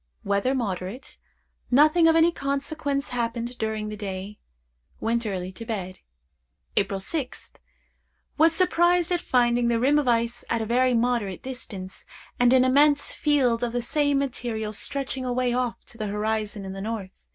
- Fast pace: No, average, 160 wpm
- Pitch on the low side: No, high, 240 Hz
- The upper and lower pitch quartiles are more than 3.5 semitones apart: Yes, average, 4.4 semitones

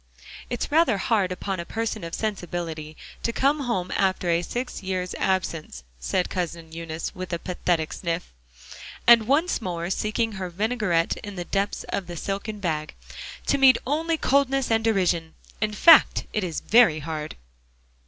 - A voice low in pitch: No, high, 190 Hz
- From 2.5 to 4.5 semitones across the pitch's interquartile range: No, average, 5.0 semitones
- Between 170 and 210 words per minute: No, average, 160 wpm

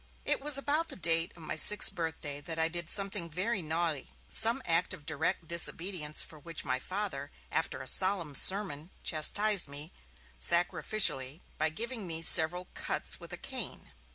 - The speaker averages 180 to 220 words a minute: No, average, 165 wpm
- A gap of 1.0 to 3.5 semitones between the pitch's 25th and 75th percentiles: No, average, 4.1 semitones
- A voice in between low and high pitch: Yes, medium, 170 Hz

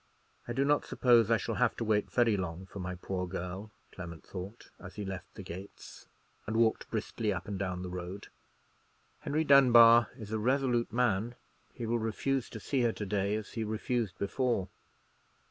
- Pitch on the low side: Yes, low, 110 Hz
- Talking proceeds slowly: No, average, 185 wpm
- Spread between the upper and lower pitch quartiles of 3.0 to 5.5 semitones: Yes, average, 3.8 semitones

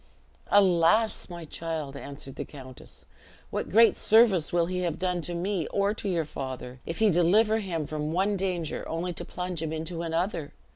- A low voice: No, medium, 170 Hz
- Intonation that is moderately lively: Yes, average, 3.3 semitones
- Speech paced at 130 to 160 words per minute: No, average, 180 wpm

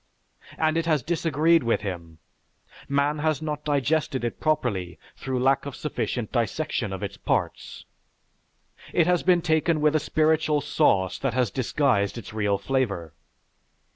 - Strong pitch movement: Yes, wide, 6.1 semitones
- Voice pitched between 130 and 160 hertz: Yes, medium, 140 Hz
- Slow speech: No, average, 145 wpm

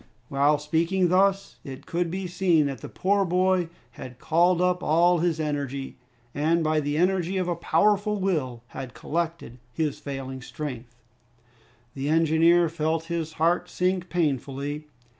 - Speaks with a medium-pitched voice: Yes, medium, 165 Hz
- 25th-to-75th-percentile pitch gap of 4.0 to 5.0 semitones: No, average, 3.6 semitones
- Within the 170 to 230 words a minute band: No, average, 145 wpm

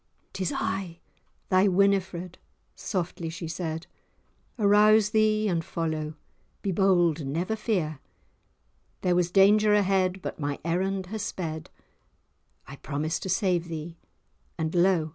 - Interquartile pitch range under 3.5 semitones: Yes, average, 3.1 semitones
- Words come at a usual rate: No, slow, 125 wpm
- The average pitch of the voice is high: No, medium, 180 Hz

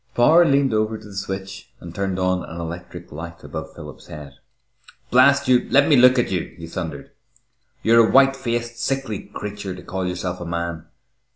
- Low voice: Yes, low, 100 Hz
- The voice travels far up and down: Yes, wide, 5.7 semitones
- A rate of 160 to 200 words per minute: Yes, average, 185 wpm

